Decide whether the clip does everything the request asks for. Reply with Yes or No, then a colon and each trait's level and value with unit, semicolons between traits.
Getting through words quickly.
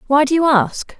Yes: fast, 240 wpm